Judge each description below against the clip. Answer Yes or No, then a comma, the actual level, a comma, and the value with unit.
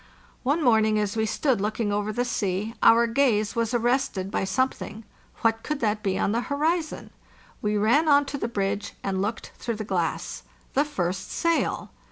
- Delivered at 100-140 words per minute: No, average, 185 wpm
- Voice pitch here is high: Yes, high, 225 Hz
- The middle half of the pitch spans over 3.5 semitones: Yes, average, 4.0 semitones